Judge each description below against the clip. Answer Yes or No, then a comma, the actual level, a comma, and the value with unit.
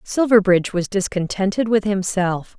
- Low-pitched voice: No, high, 195 Hz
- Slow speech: Yes, slow, 115 wpm